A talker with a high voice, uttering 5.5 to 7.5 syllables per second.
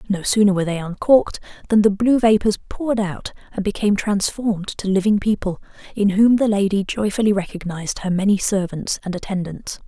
Yes: high, 200 Hz; 5.8 syllables/s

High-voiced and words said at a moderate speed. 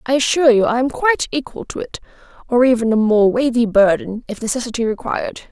Yes: high, 245 Hz; average, 195 wpm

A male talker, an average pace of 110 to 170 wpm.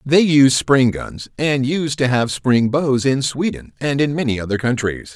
No: male; average, 200 wpm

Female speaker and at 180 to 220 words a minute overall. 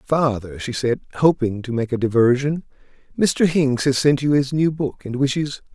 No: male; average, 190 wpm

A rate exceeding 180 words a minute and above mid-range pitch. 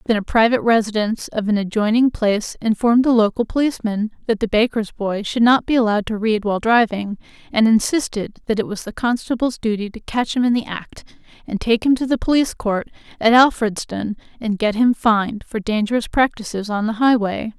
Yes: average, 195 wpm; high, 225 Hz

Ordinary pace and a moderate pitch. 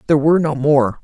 No: fast, 235 wpm; medium, 150 Hz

